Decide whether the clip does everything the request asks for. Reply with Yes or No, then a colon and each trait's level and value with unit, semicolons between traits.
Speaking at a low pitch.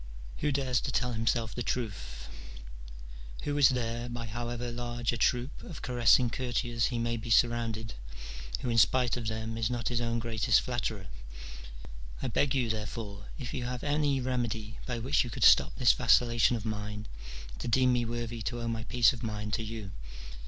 Yes: low, 120 Hz